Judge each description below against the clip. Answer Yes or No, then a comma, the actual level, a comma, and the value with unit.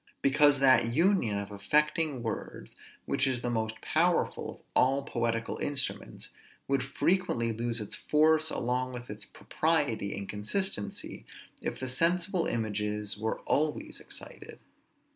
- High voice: No, low, 125 Hz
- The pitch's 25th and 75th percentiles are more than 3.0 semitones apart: Yes, average, 5.3 semitones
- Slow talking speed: Yes, slow, 130 wpm